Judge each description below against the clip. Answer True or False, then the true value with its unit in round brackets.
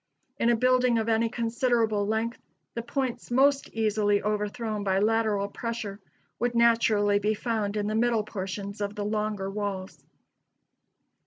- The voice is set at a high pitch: True (220 Hz)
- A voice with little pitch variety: True (2.2 semitones)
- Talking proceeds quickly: False (145 wpm)